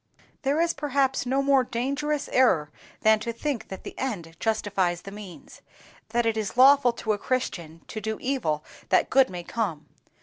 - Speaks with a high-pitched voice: Yes, high, 230 Hz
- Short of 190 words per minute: Yes, average, 170 wpm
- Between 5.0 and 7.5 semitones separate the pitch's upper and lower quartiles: Yes, average, 5.3 semitones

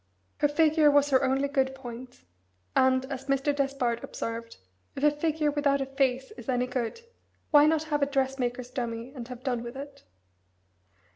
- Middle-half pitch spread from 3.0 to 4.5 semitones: No, narrow, 2.5 semitones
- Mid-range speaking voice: No, very high, 270 Hz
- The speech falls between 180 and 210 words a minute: No, average, 170 wpm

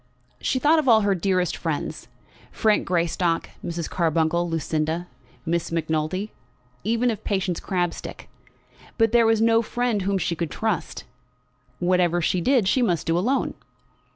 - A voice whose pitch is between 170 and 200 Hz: Yes, medium, 185 Hz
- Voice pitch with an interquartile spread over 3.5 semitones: Yes, average, 4.9 semitones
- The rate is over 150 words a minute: No, average, 145 wpm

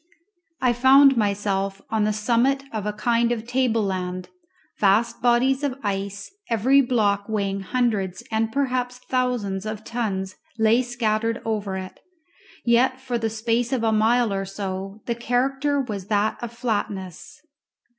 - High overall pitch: Yes, high, 225 Hz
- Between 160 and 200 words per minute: No, average, 145 wpm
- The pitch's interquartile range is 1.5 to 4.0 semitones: Yes, average, 3.6 semitones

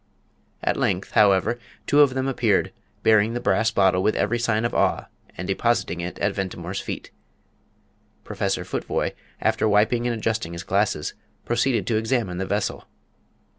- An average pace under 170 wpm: Yes, average, 155 wpm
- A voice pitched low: Yes, low, 110 Hz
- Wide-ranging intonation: No, average, 3.6 semitones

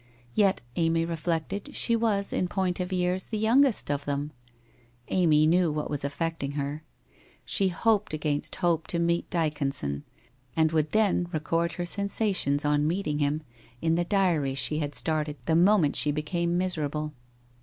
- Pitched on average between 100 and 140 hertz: No, medium, 165 Hz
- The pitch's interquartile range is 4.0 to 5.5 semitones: No, average, 3.6 semitones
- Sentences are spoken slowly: No, average, 160 wpm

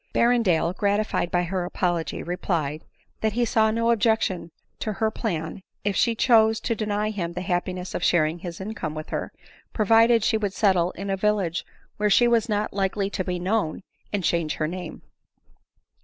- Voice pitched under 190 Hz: No, high, 195 Hz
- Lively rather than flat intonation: No, average, 3.9 semitones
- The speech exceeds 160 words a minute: Yes, average, 180 wpm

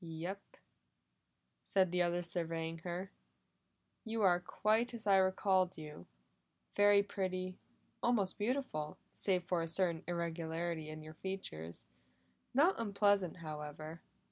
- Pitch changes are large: No, average, 3.4 semitones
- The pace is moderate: No, slow, 115 wpm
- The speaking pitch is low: No, medium, 180 Hz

